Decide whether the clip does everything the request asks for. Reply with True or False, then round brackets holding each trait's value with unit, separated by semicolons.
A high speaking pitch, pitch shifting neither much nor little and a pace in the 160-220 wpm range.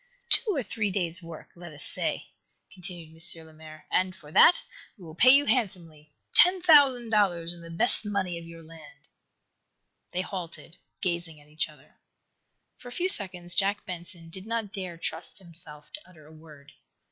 False (175 Hz; 4.0 semitones; 175 wpm)